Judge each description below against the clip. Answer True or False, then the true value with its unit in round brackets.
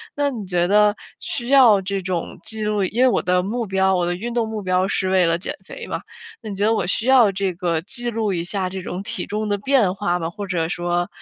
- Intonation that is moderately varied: True (3.3 semitones)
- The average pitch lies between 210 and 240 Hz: False (195 Hz)